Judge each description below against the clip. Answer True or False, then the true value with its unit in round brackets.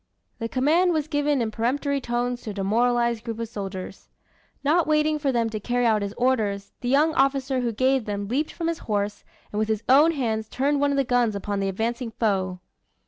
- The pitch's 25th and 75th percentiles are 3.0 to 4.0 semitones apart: False (4.5 semitones)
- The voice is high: True (240 Hz)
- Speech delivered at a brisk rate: True (210 wpm)